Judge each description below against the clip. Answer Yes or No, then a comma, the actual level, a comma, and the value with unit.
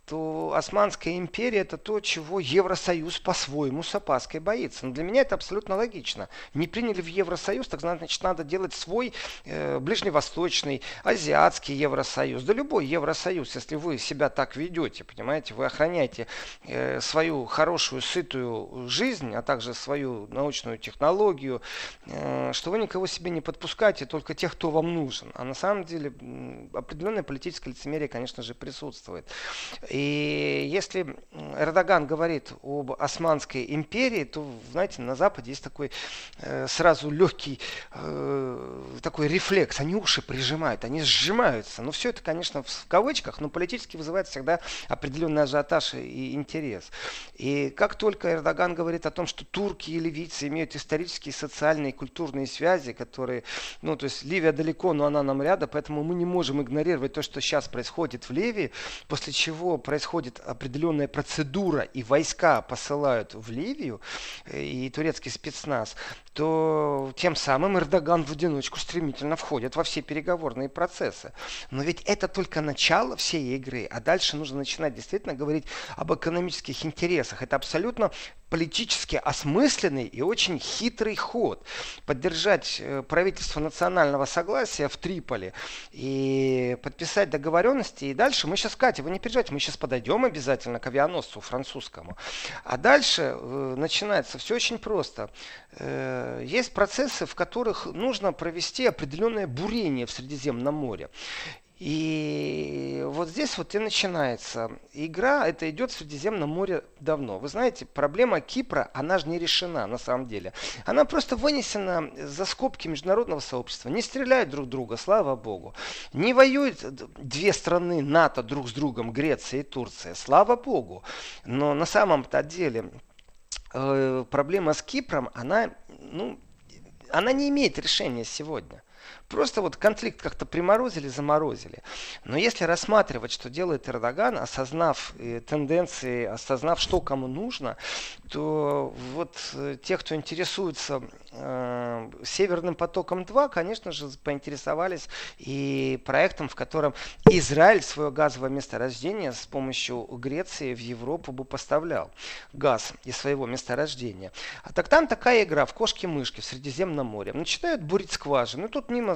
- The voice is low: No, medium, 155 Hz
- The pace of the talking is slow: No, average, 135 wpm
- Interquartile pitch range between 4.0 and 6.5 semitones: Yes, average, 5.1 semitones